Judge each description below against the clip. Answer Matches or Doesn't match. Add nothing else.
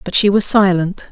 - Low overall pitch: Doesn't match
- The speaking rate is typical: Doesn't match